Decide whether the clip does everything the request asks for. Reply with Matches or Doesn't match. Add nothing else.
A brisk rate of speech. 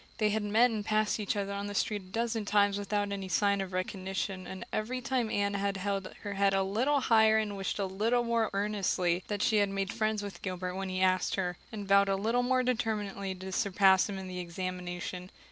Matches